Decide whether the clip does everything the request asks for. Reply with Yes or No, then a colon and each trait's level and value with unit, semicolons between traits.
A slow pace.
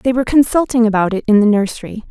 No: fast, 230 wpm